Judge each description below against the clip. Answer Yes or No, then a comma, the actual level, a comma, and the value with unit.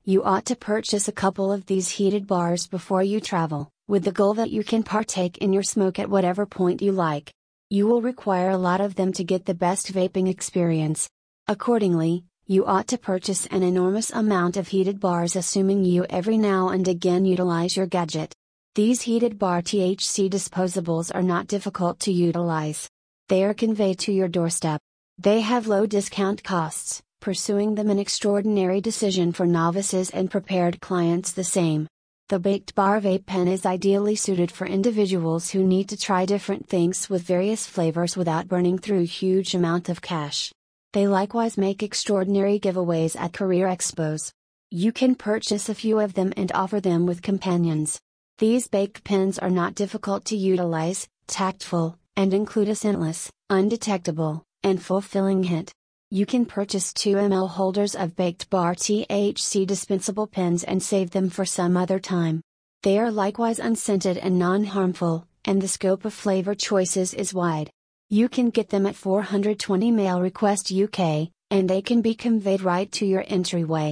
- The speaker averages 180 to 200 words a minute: No, average, 170 wpm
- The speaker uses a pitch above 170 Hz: Yes, high, 190 Hz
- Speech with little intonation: Yes, narrow, 2.1 semitones